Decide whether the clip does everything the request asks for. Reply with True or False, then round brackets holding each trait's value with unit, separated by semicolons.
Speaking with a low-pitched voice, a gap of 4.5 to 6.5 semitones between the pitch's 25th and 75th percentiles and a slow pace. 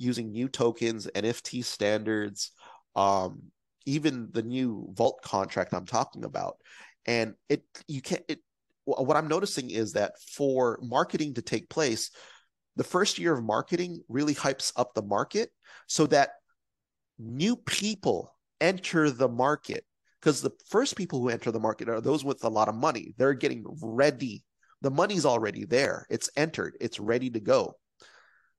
False (130 Hz; 5.5 semitones; 155 wpm)